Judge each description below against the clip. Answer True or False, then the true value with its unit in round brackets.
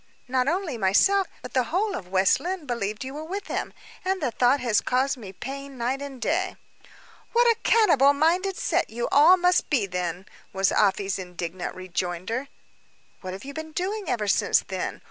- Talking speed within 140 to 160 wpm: False (185 wpm)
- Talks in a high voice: True (265 Hz)